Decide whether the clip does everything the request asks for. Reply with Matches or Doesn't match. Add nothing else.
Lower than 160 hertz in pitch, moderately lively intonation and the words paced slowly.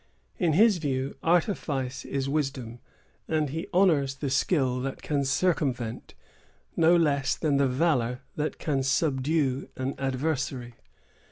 Matches